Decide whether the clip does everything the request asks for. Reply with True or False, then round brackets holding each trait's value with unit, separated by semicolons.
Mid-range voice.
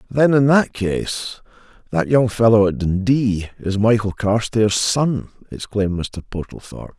False (110 Hz)